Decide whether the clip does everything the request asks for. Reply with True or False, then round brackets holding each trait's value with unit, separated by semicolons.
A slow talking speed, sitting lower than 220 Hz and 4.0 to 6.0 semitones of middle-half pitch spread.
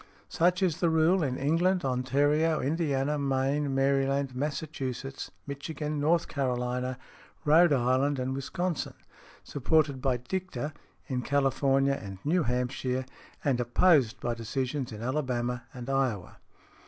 False (120 wpm; 135 Hz; 3.1 semitones)